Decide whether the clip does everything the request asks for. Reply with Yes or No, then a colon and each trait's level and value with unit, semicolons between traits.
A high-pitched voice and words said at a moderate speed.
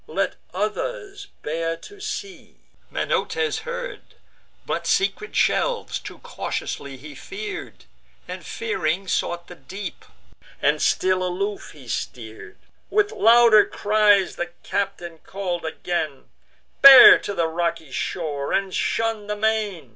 No: high, 195 Hz; slow, 120 wpm